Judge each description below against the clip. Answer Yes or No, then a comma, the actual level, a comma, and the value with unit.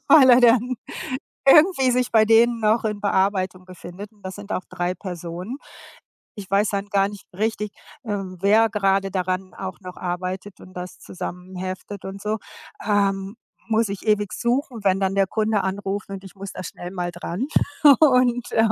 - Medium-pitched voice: No, high, 200 Hz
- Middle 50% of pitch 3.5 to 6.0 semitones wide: No, average, 2.9 semitones